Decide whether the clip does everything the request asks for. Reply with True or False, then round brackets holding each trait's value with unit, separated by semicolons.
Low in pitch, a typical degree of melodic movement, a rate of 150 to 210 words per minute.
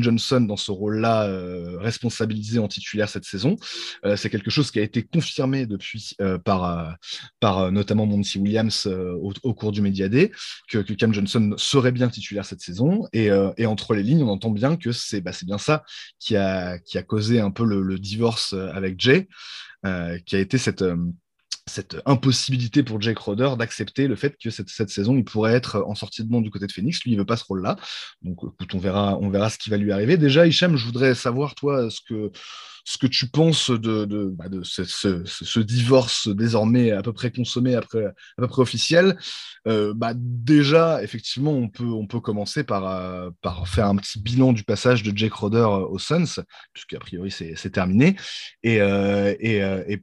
False (110 Hz; 3.7 semitones; 220 wpm)